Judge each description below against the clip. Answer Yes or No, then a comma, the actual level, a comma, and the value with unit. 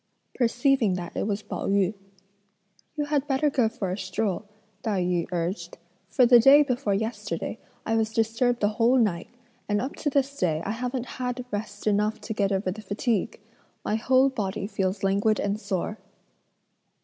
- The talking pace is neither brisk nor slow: Yes, average, 175 wpm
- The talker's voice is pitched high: Yes, high, 220 Hz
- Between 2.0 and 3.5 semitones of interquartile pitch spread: No, average, 4.0 semitones